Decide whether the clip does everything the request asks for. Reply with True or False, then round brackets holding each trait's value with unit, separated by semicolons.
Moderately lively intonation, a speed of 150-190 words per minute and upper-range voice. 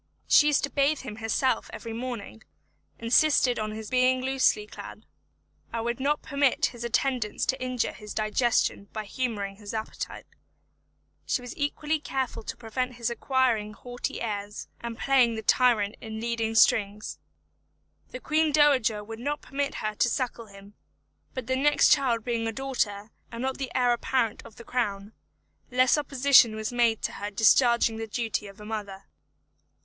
True (3.2 semitones; 165 wpm; 235 Hz)